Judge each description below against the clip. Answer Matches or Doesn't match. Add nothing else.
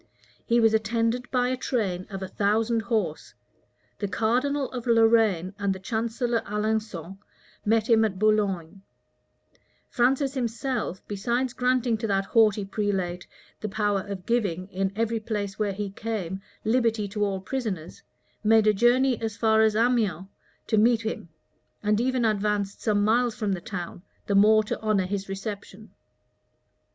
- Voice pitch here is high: Matches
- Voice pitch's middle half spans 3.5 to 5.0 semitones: Doesn't match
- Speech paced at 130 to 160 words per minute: Matches